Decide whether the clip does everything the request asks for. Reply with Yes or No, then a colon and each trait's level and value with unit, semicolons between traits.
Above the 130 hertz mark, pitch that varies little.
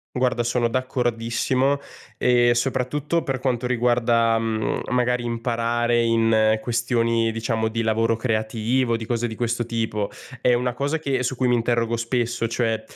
No: low, 120 Hz; narrow, 1.5 semitones